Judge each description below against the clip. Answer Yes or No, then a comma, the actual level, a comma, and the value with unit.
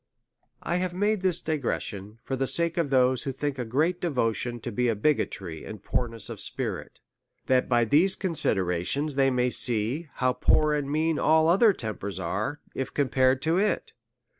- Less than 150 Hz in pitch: Yes, low, 135 Hz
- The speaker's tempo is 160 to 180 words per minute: Yes, average, 170 wpm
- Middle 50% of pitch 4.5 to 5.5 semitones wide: Yes, average, 5.2 semitones